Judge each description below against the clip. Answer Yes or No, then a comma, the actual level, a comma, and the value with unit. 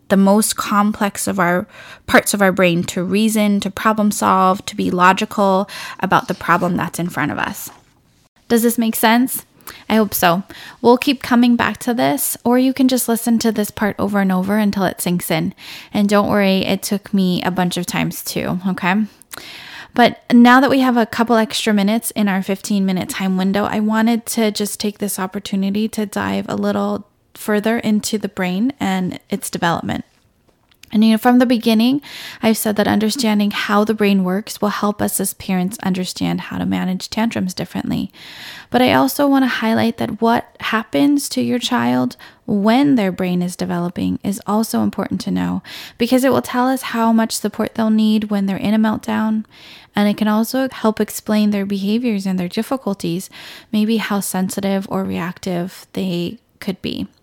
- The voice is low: No, high, 210 Hz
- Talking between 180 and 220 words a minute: Yes, average, 190 wpm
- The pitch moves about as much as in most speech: Yes, average, 3.1 semitones